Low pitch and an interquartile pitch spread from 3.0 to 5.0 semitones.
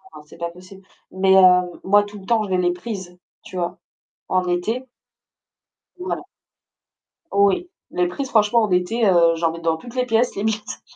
No: high, 190 Hz; average, 3.7 semitones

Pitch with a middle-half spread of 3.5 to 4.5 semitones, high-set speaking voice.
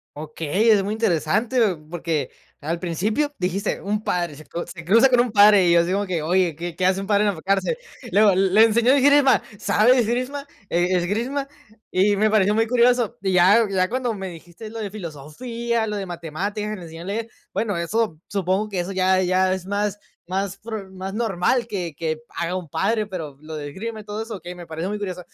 Yes: average, 3.9 semitones; high, 195 Hz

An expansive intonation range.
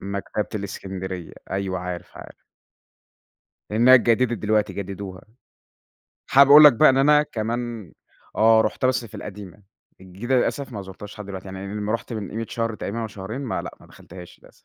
No: average, 3.7 semitones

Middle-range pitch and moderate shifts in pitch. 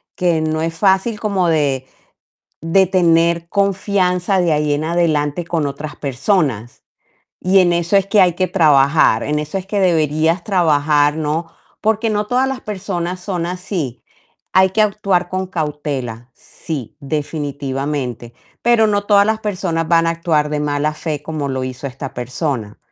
Yes: medium, 165 Hz; average, 4.3 semitones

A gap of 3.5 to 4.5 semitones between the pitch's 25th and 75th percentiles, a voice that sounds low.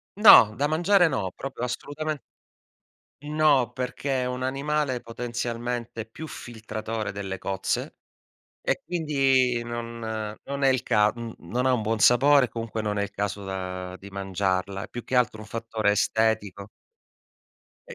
Yes: average, 3.9 semitones; low, 115 Hz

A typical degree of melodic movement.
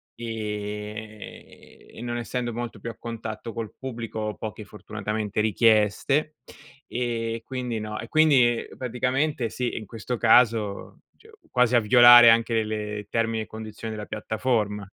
No: narrow, 2.1 semitones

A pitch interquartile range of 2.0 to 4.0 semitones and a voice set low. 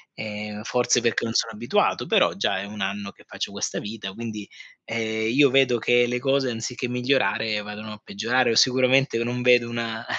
Yes: narrow, 2.5 semitones; low, 115 Hz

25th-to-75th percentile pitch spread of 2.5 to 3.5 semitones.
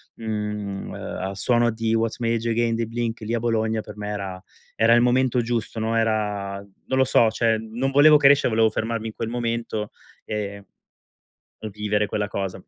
No: narrow, 1.9 semitones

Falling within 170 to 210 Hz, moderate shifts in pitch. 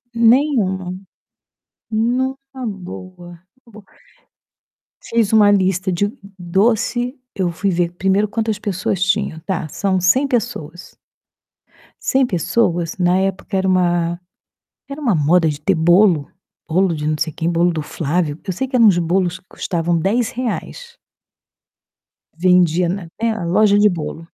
Yes: medium, 185 Hz; average, 4.1 semitones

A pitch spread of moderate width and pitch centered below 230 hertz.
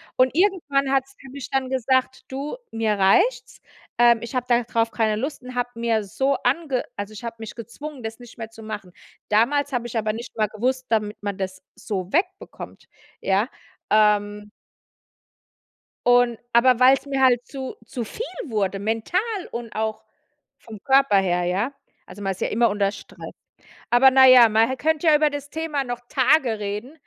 No: average, 3.8 semitones; high, 240 Hz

